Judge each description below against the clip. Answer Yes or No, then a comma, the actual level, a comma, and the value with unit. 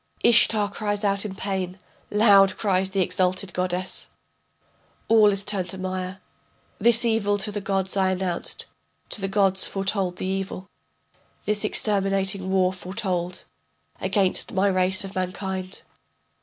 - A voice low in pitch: No, high, 195 Hz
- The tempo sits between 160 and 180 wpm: No, slow, 135 wpm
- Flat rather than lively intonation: Yes, narrow, 1.5 semitones